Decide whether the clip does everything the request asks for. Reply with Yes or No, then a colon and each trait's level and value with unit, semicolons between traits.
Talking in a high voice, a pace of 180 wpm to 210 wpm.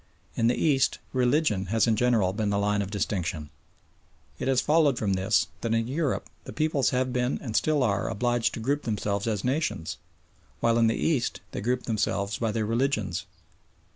No: low, 115 Hz; average, 185 wpm